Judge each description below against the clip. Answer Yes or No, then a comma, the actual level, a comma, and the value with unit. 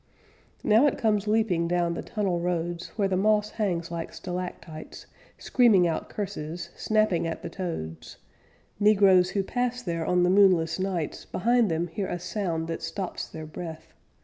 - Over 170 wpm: No, average, 160 wpm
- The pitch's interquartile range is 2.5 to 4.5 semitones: Yes, average, 3.7 semitones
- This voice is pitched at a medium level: Yes, medium, 180 Hz